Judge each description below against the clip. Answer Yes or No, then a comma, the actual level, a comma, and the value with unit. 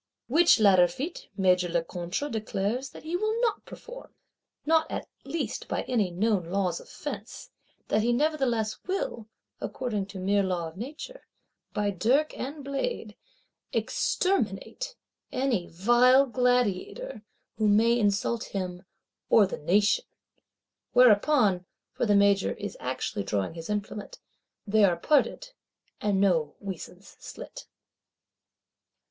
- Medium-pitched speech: No, high, 215 Hz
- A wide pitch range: Yes, wide, 6.0 semitones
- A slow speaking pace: Yes, slow, 125 wpm